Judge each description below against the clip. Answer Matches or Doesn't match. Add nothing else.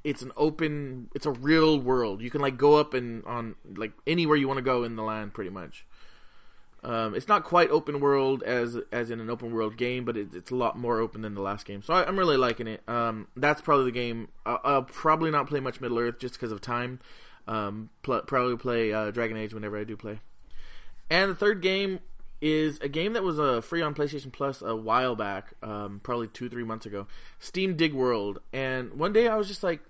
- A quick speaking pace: Matches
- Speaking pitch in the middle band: Doesn't match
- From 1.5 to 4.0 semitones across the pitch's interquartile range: Doesn't match